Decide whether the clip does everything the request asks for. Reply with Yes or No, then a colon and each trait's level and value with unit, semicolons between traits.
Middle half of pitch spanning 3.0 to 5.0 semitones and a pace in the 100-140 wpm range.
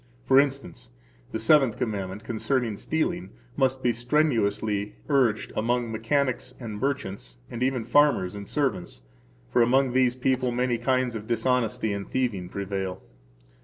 Yes: average, 3.9 semitones; slow, 135 wpm